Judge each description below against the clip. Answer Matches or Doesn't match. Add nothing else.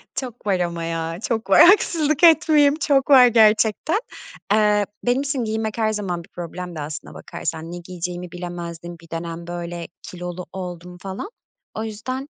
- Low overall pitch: Doesn't match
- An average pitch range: Doesn't match